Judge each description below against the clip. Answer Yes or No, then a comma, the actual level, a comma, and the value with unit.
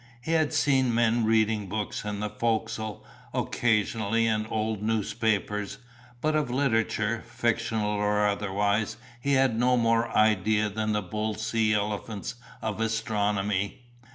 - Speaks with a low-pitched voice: Yes, low, 110 Hz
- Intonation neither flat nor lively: No, narrow, 1.7 semitones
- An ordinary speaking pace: No, slow, 130 wpm